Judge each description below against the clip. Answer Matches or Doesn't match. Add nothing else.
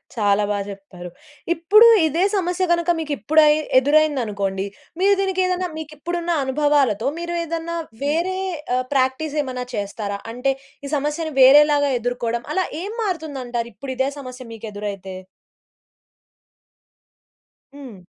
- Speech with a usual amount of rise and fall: Doesn't match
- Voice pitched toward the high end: Matches